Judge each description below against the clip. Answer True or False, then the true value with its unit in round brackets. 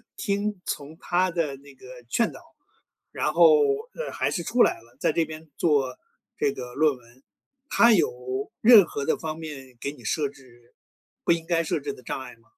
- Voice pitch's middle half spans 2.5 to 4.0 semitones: False (5.2 semitones)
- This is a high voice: False (155 Hz)